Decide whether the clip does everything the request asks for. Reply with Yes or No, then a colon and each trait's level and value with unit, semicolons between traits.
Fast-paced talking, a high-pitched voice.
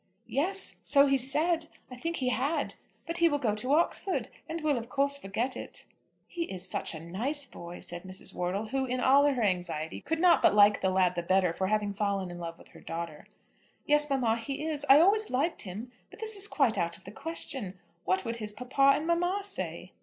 Yes: fast, 220 wpm; very high, 255 Hz